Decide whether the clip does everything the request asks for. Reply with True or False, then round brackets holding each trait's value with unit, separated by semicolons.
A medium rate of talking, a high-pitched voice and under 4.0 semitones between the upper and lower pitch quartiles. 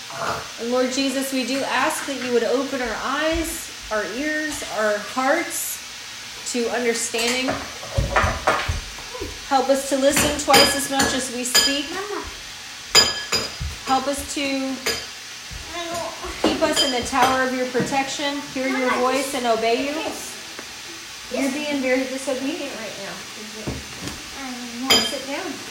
False (125 wpm; 270 Hz; 2.4 semitones)